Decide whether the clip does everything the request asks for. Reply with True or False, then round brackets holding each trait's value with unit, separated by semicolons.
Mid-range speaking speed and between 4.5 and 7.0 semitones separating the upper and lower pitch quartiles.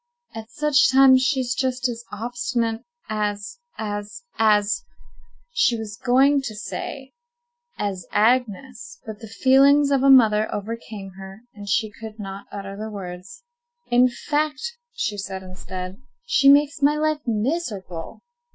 False (130 wpm; 4.9 semitones)